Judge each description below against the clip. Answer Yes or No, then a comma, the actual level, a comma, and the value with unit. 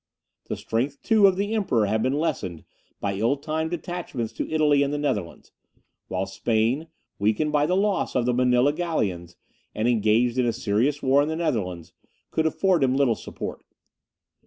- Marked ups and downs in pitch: Yes, wide, 6.2 semitones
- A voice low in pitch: Yes, low, 130 Hz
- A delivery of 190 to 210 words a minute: No, average, 175 wpm